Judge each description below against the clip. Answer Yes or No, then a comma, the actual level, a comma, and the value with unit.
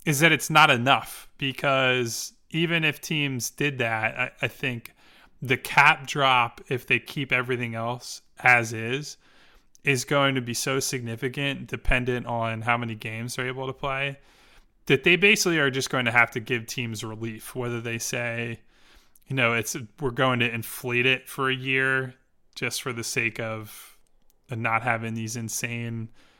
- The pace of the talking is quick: No, average, 170 wpm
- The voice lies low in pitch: Yes, low, 125 Hz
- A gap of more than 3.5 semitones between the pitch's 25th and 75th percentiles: No, average, 2.8 semitones